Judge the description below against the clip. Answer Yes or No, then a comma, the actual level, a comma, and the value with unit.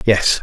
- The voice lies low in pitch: Yes, low, 105 Hz